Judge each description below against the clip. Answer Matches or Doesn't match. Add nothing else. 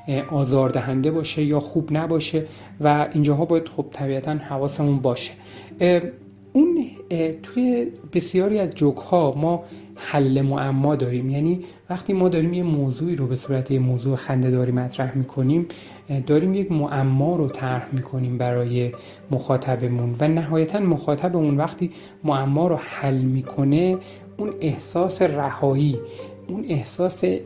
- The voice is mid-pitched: Matches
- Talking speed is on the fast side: Doesn't match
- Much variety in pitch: Doesn't match